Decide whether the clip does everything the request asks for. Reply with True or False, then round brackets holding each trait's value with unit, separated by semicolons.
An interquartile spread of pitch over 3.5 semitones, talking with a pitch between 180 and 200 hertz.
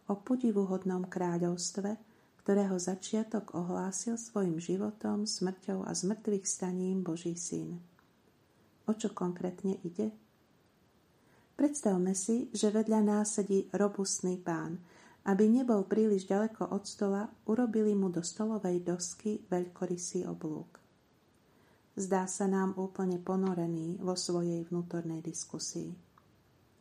False (2.8 semitones; 190 Hz)